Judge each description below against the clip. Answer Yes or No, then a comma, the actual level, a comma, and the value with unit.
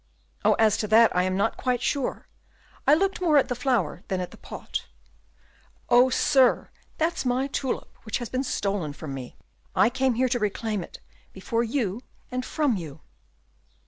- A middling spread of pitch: Yes, average, 4.8 semitones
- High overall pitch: Yes, high, 235 Hz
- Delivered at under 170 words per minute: No, average, 175 wpm